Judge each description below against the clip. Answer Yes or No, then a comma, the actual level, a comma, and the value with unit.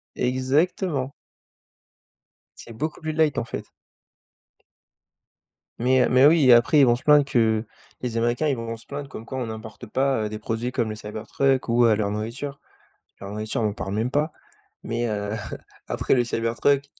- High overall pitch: No, low, 120 Hz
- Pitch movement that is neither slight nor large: Yes, average, 3.8 semitones